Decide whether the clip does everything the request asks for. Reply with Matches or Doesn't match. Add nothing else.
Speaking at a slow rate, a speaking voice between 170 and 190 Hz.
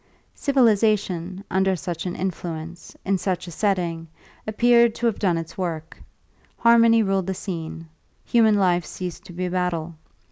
Doesn't match